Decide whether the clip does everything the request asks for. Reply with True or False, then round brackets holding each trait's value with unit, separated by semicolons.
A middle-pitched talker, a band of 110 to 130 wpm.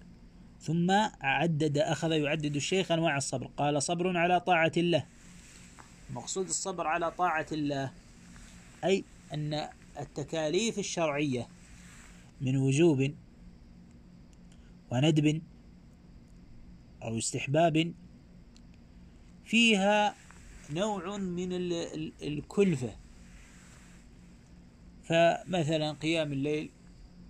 False (145 Hz; 75 wpm)